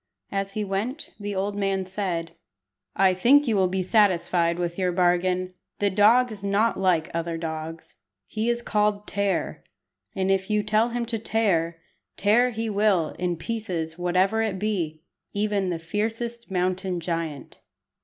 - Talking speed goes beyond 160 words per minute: No, average, 155 wpm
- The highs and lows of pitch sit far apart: No, average, 3.3 semitones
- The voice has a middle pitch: No, high, 195 Hz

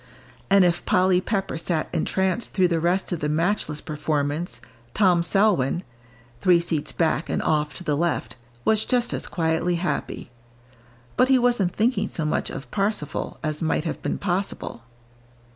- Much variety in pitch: No, average, 3.8 semitones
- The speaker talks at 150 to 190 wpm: Yes, average, 160 wpm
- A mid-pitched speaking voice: Yes, medium, 175 Hz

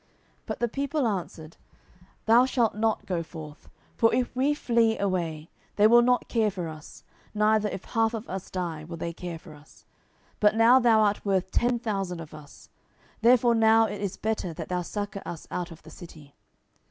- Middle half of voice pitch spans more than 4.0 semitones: Yes, average, 5.0 semitones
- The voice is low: No, high, 205 Hz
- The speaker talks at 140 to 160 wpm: No, average, 190 wpm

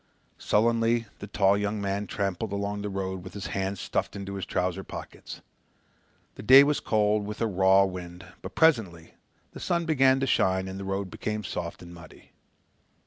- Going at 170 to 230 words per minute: Yes, average, 180 wpm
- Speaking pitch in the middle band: No, low, 100 Hz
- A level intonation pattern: Yes, narrow, 2.3 semitones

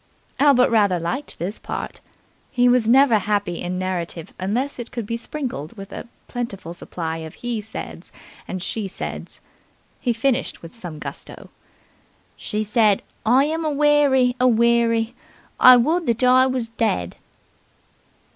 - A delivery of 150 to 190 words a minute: No, average, 140 wpm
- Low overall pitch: No, high, 230 Hz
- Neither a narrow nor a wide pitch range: Yes, average, 4.6 semitones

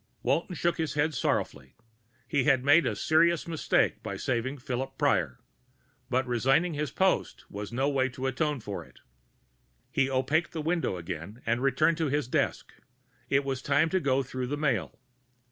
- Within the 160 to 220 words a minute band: Yes, average, 170 wpm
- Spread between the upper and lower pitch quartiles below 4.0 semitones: Yes, average, 3.5 semitones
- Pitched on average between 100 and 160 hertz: Yes, low, 135 Hz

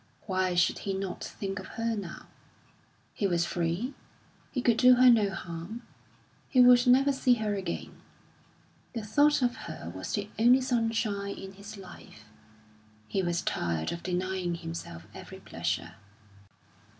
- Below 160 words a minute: Yes, average, 150 wpm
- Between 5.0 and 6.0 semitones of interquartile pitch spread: Yes, average, 5.3 semitones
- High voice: Yes, high, 200 Hz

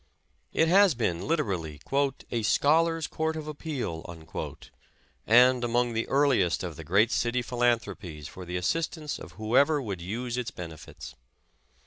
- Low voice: Yes, low, 120 Hz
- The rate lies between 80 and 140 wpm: Yes, slow, 135 wpm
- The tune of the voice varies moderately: No, wide, 8.4 semitones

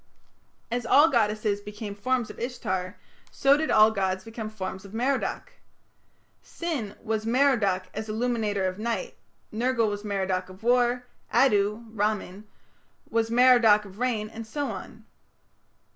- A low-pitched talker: No, high, 220 Hz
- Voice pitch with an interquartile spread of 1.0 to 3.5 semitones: Yes, average, 3.2 semitones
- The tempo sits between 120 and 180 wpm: Yes, slow, 135 wpm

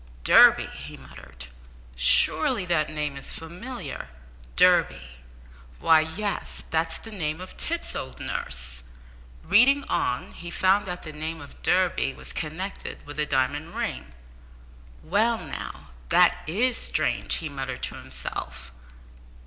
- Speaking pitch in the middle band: Yes, medium, 160 Hz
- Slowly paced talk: Yes, slow, 130 wpm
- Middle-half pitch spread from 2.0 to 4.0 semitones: No, average, 5.1 semitones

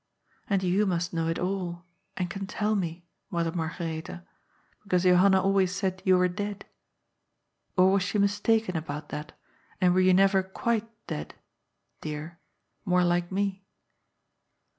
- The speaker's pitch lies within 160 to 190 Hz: Yes, medium, 185 Hz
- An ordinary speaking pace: Yes, average, 150 wpm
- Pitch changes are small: Yes, narrow, 2.3 semitones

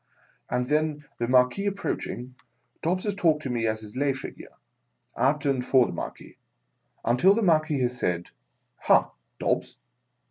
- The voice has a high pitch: No, low, 135 Hz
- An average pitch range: Yes, average, 4.1 semitones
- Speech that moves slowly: No, average, 155 wpm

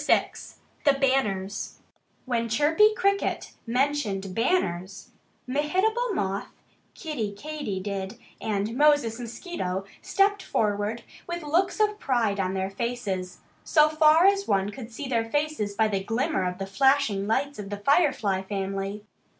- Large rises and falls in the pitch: Yes, wide, 7.2 semitones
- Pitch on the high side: Yes, high, 230 Hz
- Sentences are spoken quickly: No, slow, 135 wpm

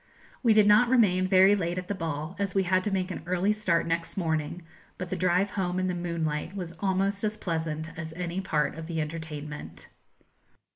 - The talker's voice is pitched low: No, medium, 180 Hz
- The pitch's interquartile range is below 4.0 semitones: Yes, average, 3.0 semitones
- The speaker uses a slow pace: No, average, 200 wpm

